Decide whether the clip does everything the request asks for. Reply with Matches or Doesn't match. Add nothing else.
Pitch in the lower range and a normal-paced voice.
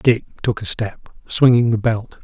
Matches